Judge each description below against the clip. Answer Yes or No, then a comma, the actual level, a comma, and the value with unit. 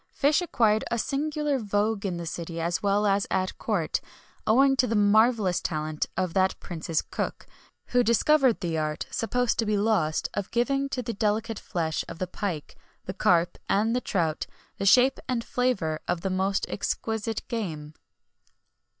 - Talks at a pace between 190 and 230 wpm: No, average, 165 wpm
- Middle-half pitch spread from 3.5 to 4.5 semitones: No, average, 5.2 semitones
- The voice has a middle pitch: No, high, 205 Hz